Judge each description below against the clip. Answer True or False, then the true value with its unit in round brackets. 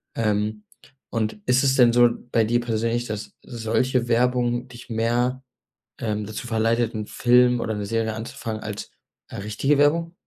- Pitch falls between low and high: False (115 Hz)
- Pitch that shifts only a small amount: True (2.1 semitones)